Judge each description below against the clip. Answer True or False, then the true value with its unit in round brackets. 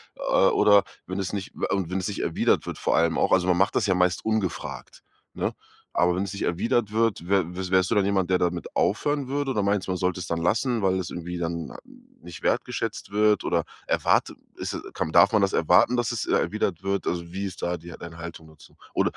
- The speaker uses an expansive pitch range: False (2.8 semitones)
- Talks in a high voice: False (95 Hz)